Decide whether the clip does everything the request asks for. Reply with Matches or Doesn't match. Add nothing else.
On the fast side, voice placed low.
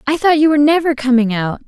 Doesn't match